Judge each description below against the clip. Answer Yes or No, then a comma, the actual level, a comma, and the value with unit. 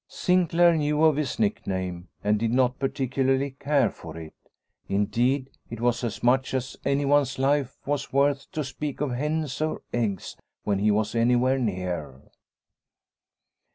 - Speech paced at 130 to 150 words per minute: Yes, average, 145 wpm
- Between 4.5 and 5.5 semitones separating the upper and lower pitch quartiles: Yes, average, 4.8 semitones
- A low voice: Yes, low, 130 Hz